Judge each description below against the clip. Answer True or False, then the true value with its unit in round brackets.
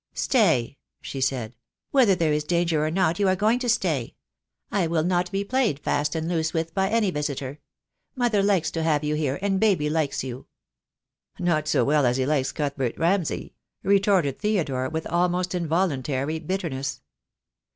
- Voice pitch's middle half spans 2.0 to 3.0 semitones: False (4.7 semitones)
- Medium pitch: True (160 Hz)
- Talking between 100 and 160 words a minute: False (170 wpm)